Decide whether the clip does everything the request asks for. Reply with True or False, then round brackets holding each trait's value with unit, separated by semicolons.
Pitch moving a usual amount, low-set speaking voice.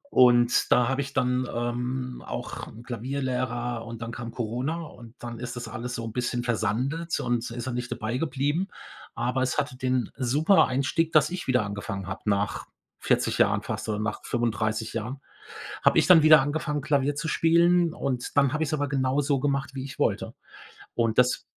True (3.1 semitones; 125 Hz)